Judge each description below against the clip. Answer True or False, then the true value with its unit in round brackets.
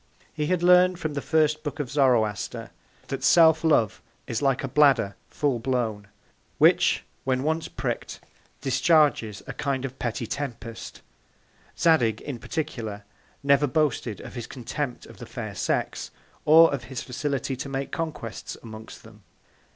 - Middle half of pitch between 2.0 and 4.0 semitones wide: False (4.6 semitones)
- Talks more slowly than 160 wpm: True (150 wpm)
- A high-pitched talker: False (135 Hz)